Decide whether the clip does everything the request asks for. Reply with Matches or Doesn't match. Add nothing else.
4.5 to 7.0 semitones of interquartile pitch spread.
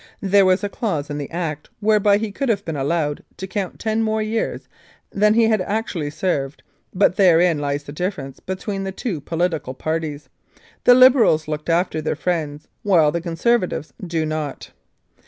Matches